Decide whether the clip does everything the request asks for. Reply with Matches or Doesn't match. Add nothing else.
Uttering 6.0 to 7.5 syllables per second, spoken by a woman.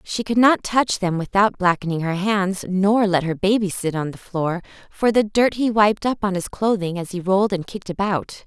Doesn't match